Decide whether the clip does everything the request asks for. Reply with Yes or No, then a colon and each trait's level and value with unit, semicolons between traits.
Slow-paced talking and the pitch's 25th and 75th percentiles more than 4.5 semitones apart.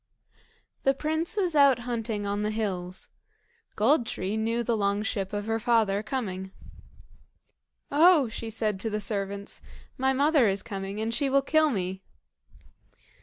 No: average, 150 wpm; average, 4.9 semitones